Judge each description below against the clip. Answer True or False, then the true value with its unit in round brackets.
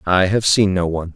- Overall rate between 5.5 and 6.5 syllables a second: True (5.8 syllables/s)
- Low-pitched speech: True (95 Hz)